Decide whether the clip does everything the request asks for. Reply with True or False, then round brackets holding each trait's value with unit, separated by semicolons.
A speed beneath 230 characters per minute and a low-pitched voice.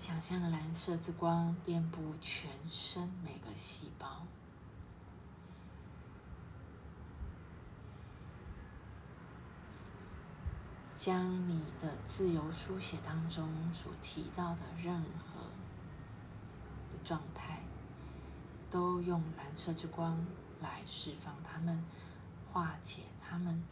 False (120 characters per minute; 160 Hz)